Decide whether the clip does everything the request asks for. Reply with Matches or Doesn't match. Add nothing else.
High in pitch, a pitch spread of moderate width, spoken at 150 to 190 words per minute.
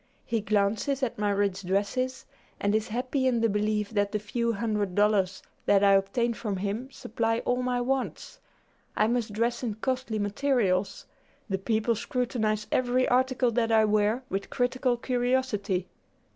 Matches